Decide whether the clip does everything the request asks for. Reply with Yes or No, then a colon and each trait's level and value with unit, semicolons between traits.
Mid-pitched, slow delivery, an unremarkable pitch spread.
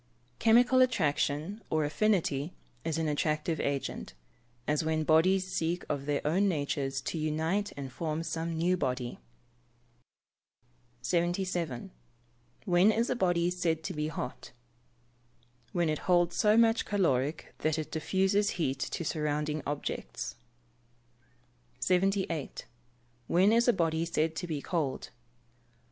Yes: medium, 165 Hz; slow, 125 wpm; average, 3.6 semitones